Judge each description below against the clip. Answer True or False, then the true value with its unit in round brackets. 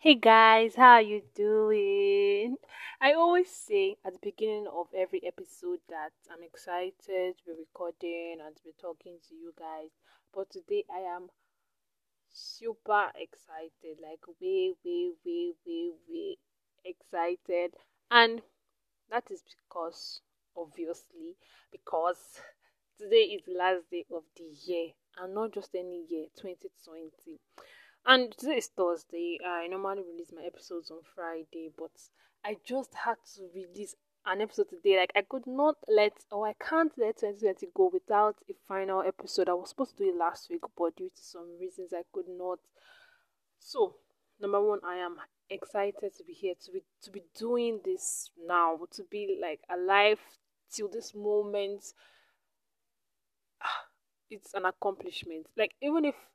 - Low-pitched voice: False (210 Hz)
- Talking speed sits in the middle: True (150 wpm)